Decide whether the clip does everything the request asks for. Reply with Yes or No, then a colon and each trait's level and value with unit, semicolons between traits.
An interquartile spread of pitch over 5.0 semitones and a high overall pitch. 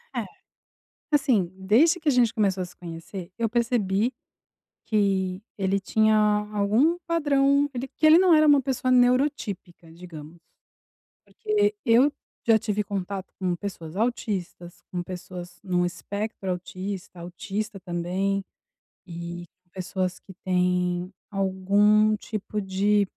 No: average, 4.6 semitones; high, 200 Hz